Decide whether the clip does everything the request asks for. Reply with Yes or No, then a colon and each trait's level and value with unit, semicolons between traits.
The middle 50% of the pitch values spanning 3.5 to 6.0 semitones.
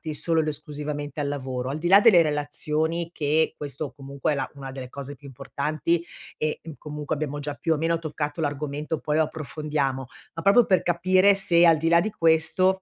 No: narrow, 2.4 semitones